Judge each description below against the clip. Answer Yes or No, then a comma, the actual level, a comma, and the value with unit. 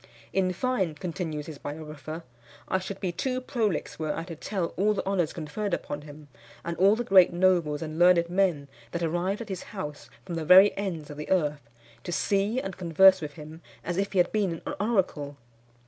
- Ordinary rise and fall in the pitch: Yes, average, 3.8 semitones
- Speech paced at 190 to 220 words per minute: Yes, average, 200 wpm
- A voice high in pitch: No, medium, 175 Hz